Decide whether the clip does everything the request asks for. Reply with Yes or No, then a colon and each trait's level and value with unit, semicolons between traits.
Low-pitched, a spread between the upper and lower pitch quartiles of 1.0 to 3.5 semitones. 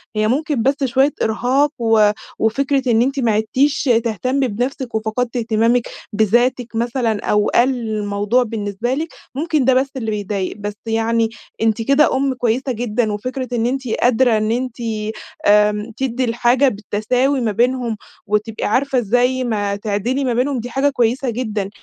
No: high, 235 Hz; average, 3.1 semitones